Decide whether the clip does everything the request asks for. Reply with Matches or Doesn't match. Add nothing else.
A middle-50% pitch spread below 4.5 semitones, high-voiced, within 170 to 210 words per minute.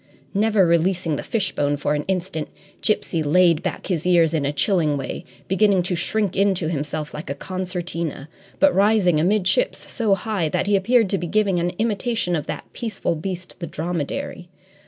Doesn't match